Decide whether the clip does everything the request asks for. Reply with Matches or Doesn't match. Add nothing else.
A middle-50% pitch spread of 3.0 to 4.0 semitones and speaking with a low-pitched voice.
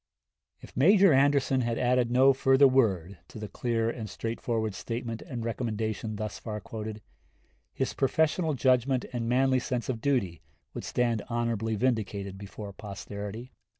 Matches